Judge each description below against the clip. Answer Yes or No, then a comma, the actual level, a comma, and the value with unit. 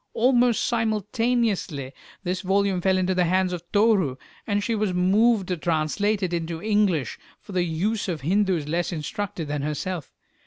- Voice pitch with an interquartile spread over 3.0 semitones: Yes, average, 3.8 semitones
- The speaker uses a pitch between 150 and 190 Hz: Yes, medium, 185 Hz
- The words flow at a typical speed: Yes, average, 160 wpm